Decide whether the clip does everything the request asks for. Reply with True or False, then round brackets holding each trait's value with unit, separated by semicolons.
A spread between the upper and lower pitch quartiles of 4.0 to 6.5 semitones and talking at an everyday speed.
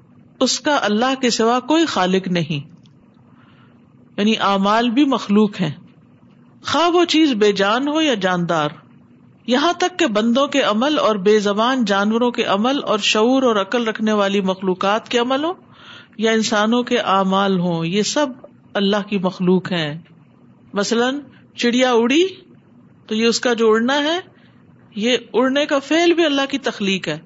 True (5.2 semitones; 160 wpm)